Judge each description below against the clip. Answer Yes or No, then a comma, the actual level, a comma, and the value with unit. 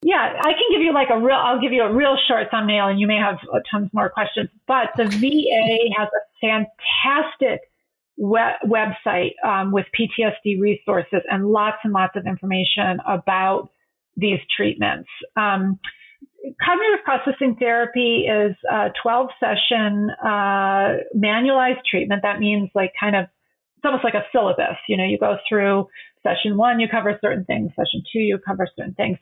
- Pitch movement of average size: Yes, average, 3.9 semitones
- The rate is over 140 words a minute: Yes, average, 165 wpm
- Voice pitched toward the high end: Yes, high, 215 Hz